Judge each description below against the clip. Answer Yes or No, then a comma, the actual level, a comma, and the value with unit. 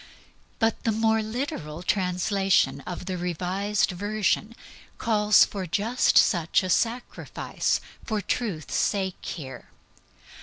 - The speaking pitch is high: Yes, high, 200 Hz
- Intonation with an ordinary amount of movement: Yes, average, 3.4 semitones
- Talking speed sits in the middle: No, slow, 110 wpm